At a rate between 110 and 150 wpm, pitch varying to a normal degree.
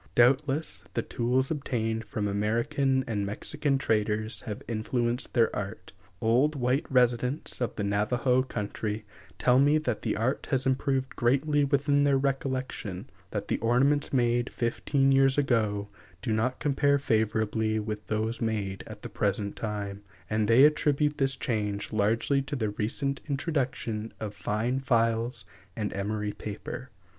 Yes: average, 145 wpm; average, 4.0 semitones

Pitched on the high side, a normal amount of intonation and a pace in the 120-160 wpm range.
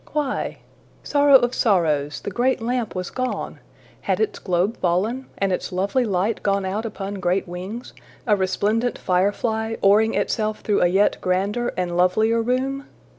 Yes: high, 205 Hz; average, 4.4 semitones; average, 155 wpm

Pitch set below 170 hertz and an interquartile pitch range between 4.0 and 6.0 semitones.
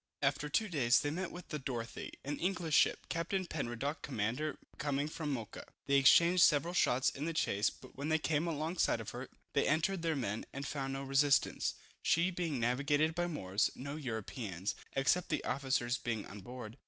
Yes: medium, 140 Hz; average, 4.3 semitones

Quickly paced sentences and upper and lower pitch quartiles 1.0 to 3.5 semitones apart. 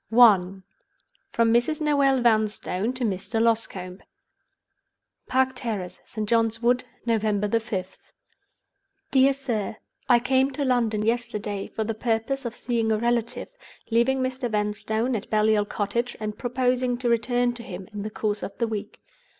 No: average, 145 wpm; narrow, 2.6 semitones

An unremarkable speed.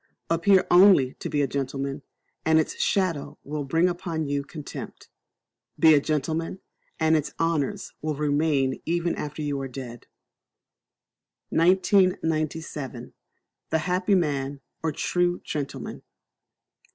No: slow, 120 wpm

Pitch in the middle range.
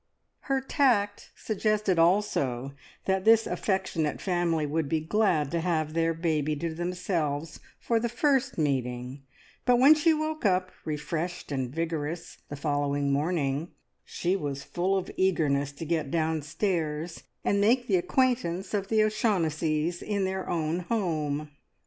Yes: medium, 170 Hz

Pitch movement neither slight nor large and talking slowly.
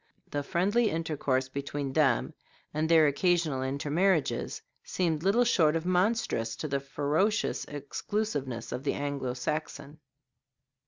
Yes: average, 4.2 semitones; slow, 120 wpm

